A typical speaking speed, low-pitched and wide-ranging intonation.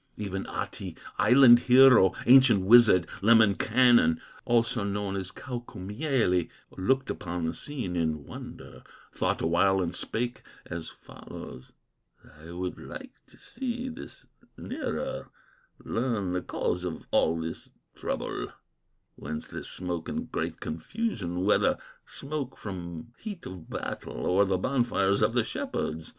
No: slow, 125 wpm; low, 100 Hz; wide, 5.8 semitones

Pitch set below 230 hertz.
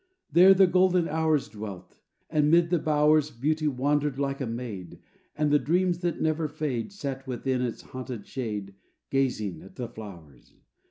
Yes: medium, 140 Hz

